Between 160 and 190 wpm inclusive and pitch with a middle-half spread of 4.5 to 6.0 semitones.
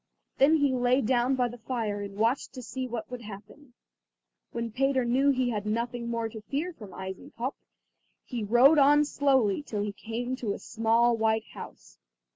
No: average, 185 wpm; average, 3.0 semitones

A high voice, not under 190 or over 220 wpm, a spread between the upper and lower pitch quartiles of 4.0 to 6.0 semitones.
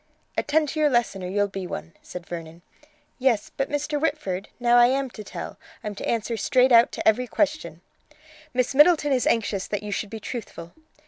Yes: high, 235 Hz; average, 195 wpm; wide, 5.4 semitones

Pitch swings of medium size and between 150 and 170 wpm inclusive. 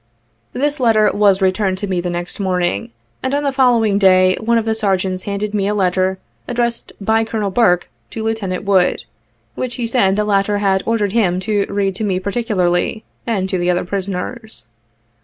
No: average, 3.1 semitones; average, 185 wpm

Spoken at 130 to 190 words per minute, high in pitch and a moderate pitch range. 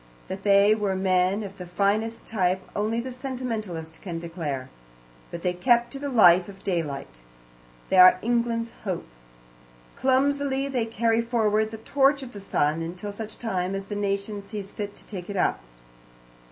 Yes: average, 165 wpm; high, 205 Hz; average, 4.1 semitones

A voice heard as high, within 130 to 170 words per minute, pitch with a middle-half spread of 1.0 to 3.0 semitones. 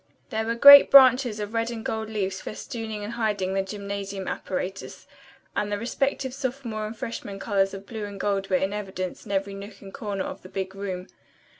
No: high, 205 Hz; average, 195 wpm; narrow, 2.6 semitones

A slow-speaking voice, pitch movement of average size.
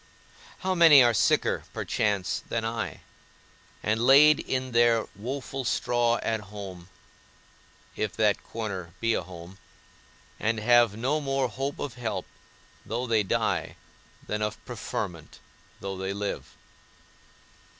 Yes: slow, 125 wpm; average, 3.8 semitones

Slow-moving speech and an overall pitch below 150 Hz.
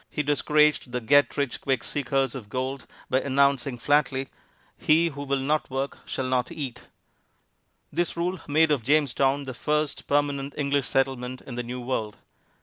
No: average, 160 wpm; medium, 140 Hz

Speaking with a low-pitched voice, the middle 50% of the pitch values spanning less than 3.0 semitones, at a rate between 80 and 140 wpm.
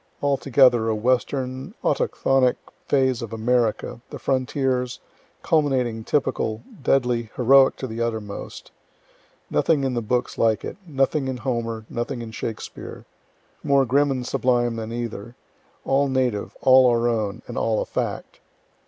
Yes: low, 125 Hz; narrow, 2.5 semitones; slow, 135 wpm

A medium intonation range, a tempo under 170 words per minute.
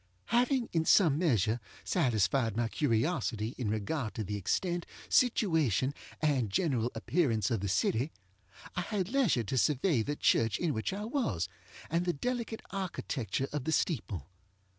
No: wide, 7.9 semitones; average, 150 wpm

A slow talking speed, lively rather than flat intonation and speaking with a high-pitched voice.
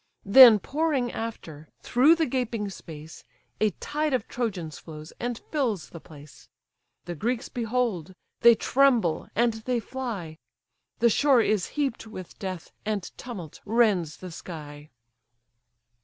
Yes: slow, 130 wpm; wide, 6.4 semitones; high, 220 Hz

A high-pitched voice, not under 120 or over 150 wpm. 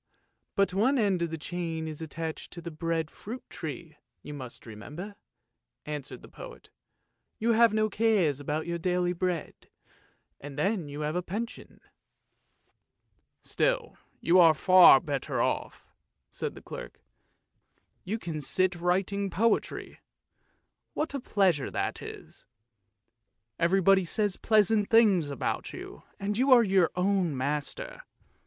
No: medium, 180 Hz; average, 140 wpm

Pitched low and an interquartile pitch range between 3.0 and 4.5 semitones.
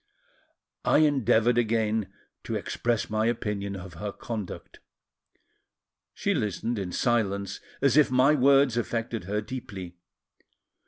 Yes: low, 110 Hz; average, 3.3 semitones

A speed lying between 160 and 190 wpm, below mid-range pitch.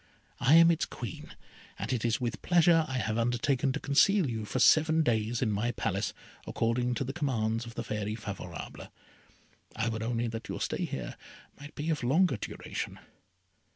Yes: average, 180 wpm; low, 120 Hz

